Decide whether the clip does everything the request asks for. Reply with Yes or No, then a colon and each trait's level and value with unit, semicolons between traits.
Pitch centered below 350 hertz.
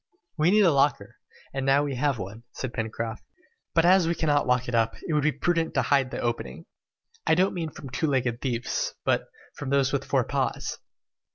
Yes: medium, 140 Hz